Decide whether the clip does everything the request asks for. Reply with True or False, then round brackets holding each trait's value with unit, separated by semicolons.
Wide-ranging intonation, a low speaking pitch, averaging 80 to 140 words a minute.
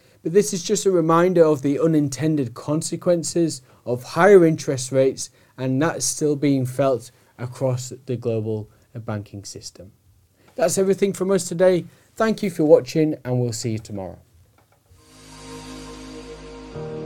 True (6.7 semitones; 130 Hz; 135 wpm)